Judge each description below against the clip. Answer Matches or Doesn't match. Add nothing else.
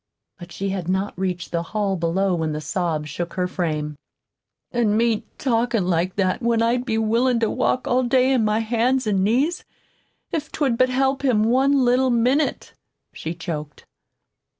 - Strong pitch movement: Matches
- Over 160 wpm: Matches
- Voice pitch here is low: Doesn't match